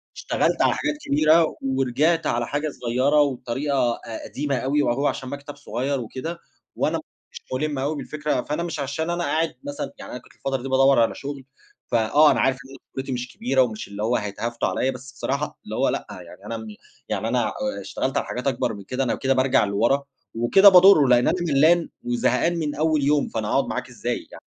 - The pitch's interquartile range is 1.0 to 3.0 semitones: No, average, 3.5 semitones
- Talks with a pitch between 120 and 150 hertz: Yes, low, 135 Hz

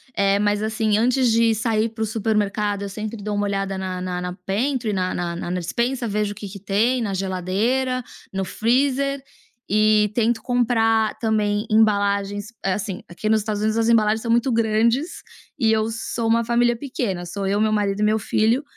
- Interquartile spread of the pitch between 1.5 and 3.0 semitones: Yes, narrow, 2.4 semitones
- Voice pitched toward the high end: Yes, high, 215 Hz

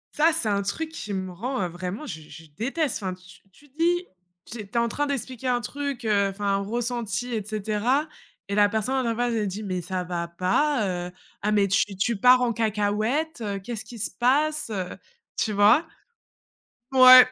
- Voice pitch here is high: Yes, high, 220 Hz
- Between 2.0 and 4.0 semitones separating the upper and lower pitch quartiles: No, average, 4.5 semitones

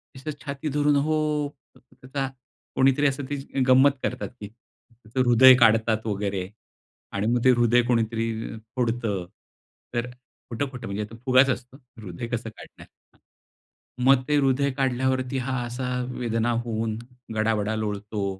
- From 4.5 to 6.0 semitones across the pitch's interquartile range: No, average, 3.1 semitones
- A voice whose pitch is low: Yes, low, 125 Hz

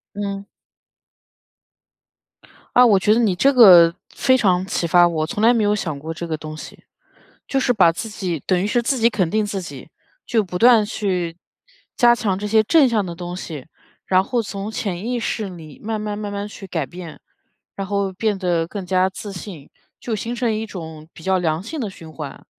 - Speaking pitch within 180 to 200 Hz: Yes, high, 195 Hz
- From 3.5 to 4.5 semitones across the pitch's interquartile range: Yes, average, 4.1 semitones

